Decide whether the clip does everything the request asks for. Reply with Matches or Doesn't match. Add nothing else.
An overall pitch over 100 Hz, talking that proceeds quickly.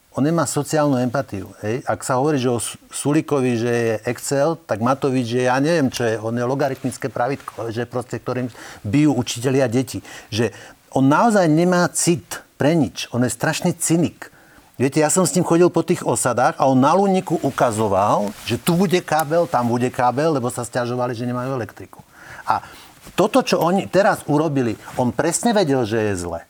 Matches